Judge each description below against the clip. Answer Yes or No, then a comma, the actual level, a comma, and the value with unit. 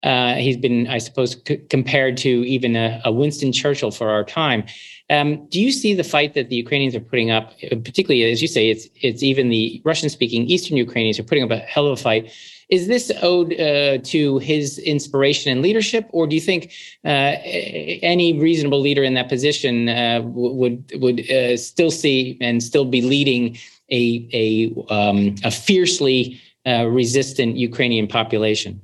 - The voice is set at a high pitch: No, low, 130 Hz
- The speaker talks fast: No, average, 180 wpm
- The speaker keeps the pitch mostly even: No, average, 3.8 semitones